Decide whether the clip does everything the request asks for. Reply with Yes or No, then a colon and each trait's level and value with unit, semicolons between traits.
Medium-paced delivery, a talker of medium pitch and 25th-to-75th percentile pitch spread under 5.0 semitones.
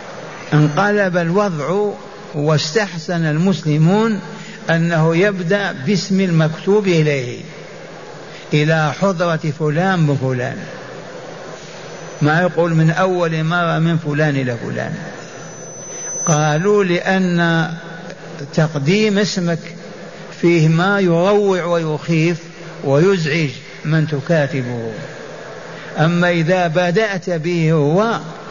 Yes: average, 80 wpm; medium, 170 Hz; average, 3.2 semitones